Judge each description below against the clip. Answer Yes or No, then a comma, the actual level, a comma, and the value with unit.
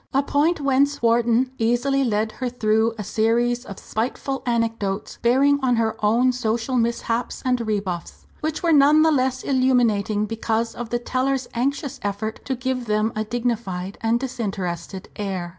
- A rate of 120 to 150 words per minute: No, average, 160 wpm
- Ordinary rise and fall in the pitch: Yes, average, 3.2 semitones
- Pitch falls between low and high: No, high, 235 Hz